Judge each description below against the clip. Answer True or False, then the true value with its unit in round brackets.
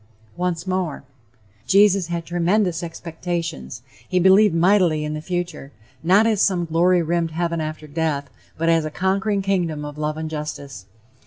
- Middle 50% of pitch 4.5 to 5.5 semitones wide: False (2.9 semitones)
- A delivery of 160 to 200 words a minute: False (150 wpm)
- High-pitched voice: False (170 Hz)